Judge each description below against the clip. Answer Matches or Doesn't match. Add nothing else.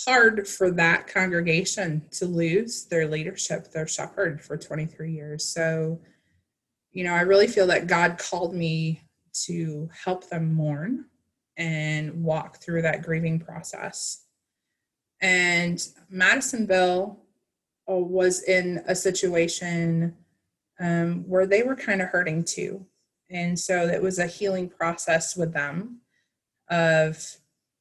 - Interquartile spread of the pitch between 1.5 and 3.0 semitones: Matches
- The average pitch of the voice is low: Doesn't match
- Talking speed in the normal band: Doesn't match